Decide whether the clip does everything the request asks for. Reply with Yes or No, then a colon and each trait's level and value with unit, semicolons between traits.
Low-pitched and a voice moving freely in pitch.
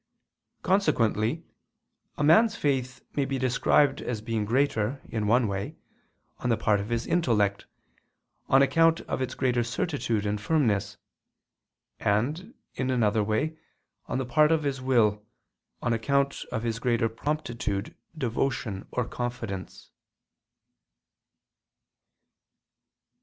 No: low, 120 Hz; average, 4.4 semitones